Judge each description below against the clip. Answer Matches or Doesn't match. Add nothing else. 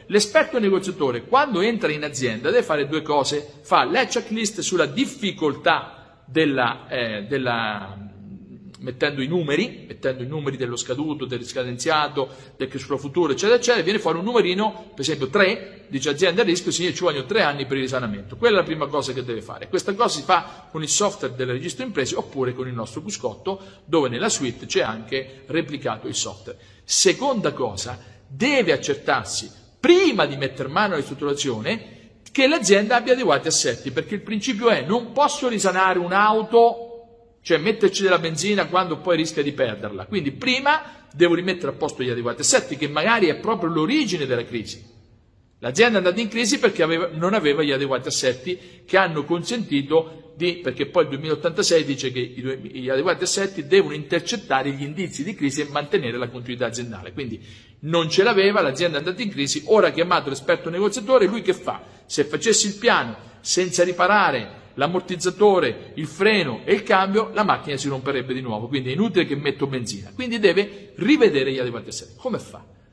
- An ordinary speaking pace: Doesn't match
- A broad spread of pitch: Matches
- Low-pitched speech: Doesn't match